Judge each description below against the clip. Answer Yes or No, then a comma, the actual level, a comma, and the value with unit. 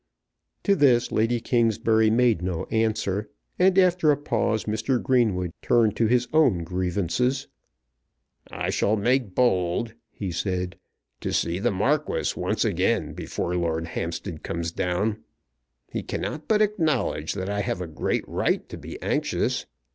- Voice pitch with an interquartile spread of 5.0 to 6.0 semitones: Yes, wide, 5.4 semitones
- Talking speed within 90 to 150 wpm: Yes, average, 145 wpm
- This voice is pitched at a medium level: No, low, 110 Hz